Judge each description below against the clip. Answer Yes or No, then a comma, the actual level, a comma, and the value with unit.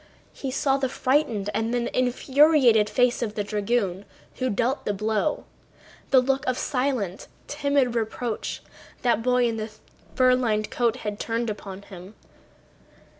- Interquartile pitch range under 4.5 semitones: Yes, average, 3.4 semitones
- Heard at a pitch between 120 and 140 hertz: No, high, 240 Hz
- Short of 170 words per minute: Yes, average, 145 wpm